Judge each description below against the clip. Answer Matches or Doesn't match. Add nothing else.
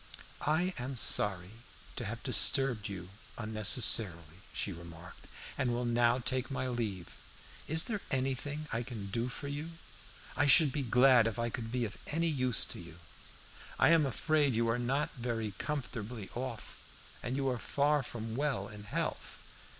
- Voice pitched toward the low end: Matches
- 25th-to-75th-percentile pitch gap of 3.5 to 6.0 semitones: Matches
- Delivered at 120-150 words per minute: Doesn't match